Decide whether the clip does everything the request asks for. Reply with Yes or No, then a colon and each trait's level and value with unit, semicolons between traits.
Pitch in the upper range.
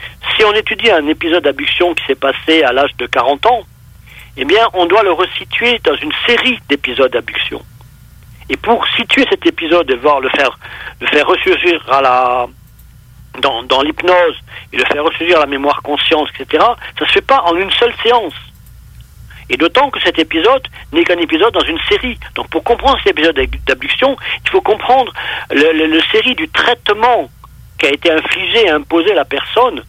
Yes: high, 215 Hz